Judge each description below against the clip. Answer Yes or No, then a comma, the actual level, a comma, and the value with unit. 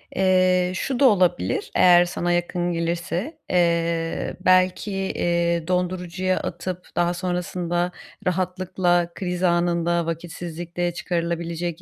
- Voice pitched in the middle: Yes, medium, 175 Hz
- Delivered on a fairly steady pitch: Yes, narrow, 1.2 semitones